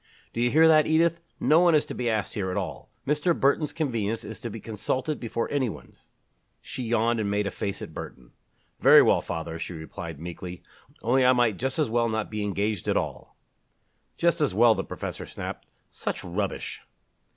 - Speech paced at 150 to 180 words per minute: No, average, 195 wpm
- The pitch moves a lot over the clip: Yes, wide, 5.7 semitones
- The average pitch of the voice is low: Yes, low, 115 Hz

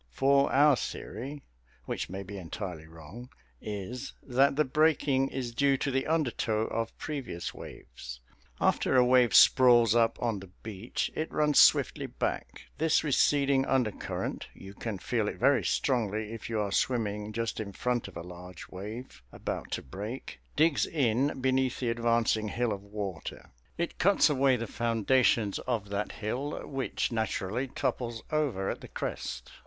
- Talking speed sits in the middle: Yes, average, 160 wpm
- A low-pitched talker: Yes, low, 120 Hz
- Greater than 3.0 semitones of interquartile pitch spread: Yes, average, 4.4 semitones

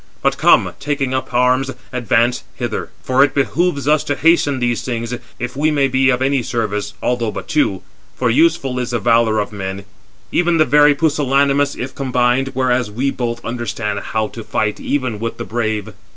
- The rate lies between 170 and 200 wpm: Yes, average, 180 wpm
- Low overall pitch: Yes, low, 125 Hz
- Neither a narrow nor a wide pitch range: Yes, average, 3.2 semitones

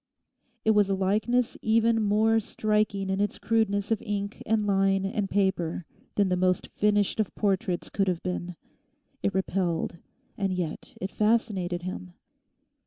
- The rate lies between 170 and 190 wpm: No, average, 150 wpm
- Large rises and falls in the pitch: No, narrow, 2.4 semitones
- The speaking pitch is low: No, high, 200 Hz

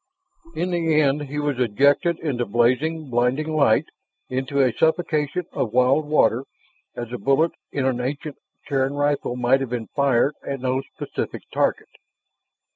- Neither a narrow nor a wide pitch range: Yes, average, 3.2 semitones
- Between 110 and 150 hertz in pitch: Yes, medium, 140 Hz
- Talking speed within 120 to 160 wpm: Yes, average, 150 wpm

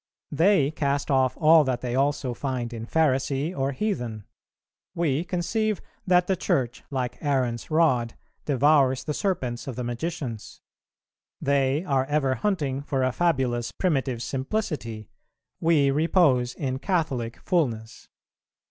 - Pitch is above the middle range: No, low, 135 Hz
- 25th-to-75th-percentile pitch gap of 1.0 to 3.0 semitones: No, average, 4.3 semitones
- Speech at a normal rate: No, slow, 130 wpm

